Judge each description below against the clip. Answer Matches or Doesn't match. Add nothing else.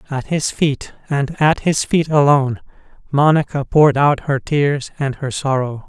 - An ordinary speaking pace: Matches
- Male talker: Matches